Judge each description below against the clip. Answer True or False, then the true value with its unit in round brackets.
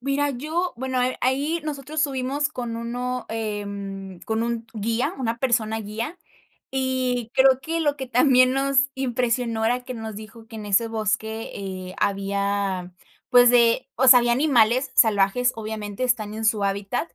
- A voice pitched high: True (235 Hz)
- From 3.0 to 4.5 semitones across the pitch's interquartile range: True (3.3 semitones)